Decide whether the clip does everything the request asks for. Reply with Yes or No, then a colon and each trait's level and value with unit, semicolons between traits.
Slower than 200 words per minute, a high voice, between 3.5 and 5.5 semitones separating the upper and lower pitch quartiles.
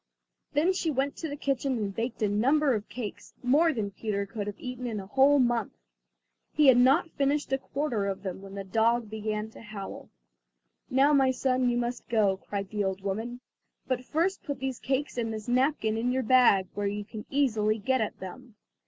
No: fast, 205 wpm; high, 240 Hz; average, 4.3 semitones